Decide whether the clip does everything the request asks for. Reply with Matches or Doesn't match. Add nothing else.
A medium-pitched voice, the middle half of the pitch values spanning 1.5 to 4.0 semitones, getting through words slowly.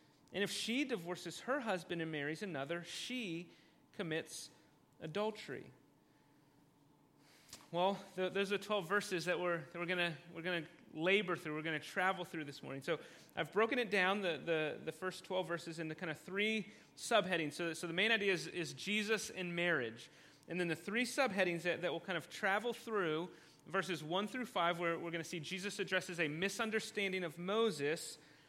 Doesn't match